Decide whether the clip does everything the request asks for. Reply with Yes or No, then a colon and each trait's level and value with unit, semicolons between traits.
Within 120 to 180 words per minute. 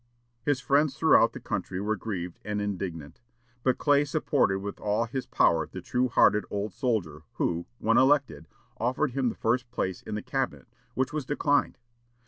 Yes: average, 170 wpm